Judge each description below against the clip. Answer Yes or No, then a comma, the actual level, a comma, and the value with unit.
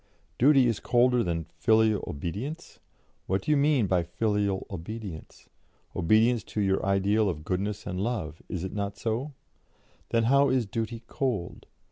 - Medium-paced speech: Yes, average, 150 wpm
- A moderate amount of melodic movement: Yes, average, 4.2 semitones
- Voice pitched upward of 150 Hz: No, low, 110 Hz